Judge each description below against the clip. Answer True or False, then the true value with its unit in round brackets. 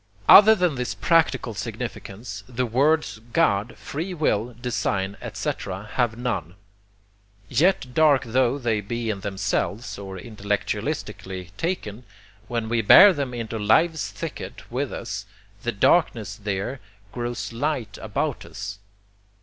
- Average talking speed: False (125 wpm)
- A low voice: True (120 Hz)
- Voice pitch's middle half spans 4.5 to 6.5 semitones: True (5.1 semitones)